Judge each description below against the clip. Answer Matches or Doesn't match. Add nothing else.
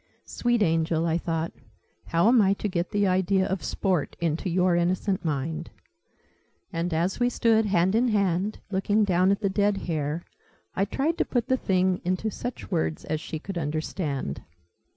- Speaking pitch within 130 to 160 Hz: Doesn't match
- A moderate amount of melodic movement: Matches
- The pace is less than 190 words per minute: Matches